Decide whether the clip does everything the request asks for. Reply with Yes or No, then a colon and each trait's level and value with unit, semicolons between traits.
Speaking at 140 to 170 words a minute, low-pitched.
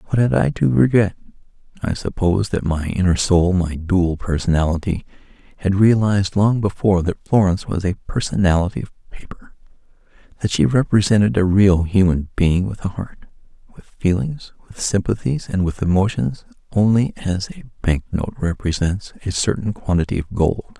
Yes: average, 145 wpm; very low, 95 Hz